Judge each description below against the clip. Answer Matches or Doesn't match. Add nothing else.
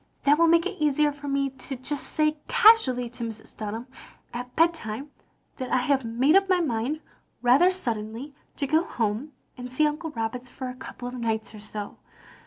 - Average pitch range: Matches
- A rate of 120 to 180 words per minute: Doesn't match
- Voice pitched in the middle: Doesn't match